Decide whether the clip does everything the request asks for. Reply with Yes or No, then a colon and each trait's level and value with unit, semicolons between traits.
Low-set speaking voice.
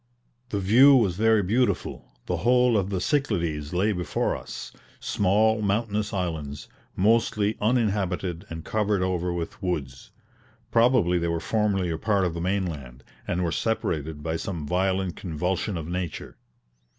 Yes: very low, 95 Hz